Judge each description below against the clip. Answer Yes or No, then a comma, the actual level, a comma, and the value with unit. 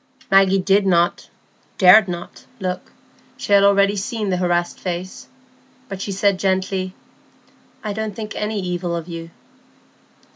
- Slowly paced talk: Yes, slow, 125 wpm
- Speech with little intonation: Yes, narrow, 1.8 semitones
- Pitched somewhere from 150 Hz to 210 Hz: Yes, high, 190 Hz